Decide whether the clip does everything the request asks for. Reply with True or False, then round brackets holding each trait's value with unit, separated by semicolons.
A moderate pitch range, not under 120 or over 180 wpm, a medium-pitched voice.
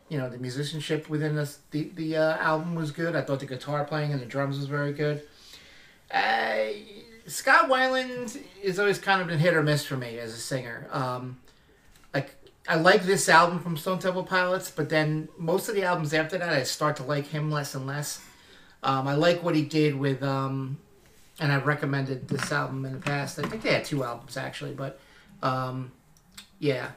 False (3.8 semitones; 205 wpm; 150 Hz)